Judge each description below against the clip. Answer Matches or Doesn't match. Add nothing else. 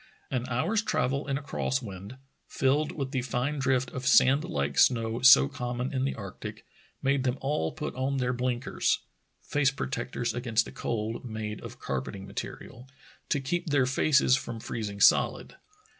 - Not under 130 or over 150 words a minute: Doesn't match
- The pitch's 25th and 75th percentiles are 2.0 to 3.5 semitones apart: Matches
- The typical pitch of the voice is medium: Doesn't match